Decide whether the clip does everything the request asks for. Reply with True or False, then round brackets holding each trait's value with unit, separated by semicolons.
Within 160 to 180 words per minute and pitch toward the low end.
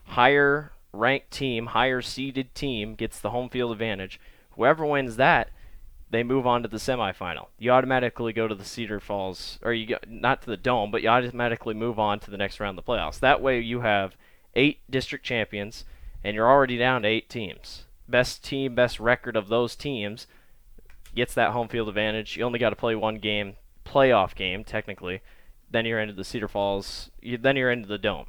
False (200 wpm; 115 Hz)